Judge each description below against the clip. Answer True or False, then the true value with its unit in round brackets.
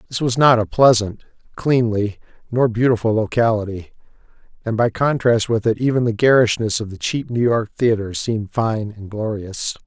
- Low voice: True (115 Hz)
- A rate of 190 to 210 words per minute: False (165 wpm)